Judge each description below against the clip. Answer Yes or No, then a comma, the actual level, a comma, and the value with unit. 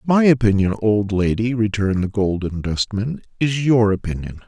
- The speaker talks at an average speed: Yes, average, 145 wpm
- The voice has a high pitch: No, low, 110 Hz